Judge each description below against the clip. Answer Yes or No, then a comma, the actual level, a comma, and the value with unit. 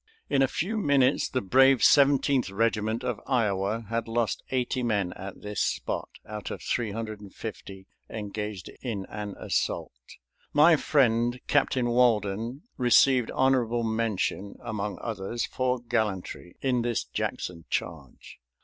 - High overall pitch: No, low, 115 Hz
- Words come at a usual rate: No, slow, 125 wpm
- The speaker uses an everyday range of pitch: Yes, average, 3.5 semitones